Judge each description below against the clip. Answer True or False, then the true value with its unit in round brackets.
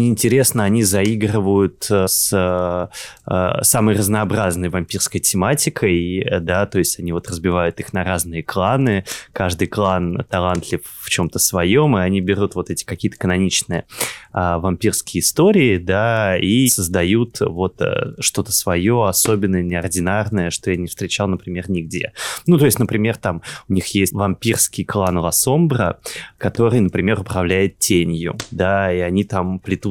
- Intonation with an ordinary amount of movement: True (3.0 semitones)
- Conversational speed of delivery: True (135 wpm)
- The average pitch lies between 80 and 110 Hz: True (95 Hz)